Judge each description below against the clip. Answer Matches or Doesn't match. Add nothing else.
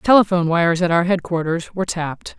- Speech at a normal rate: Matches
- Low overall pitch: Doesn't match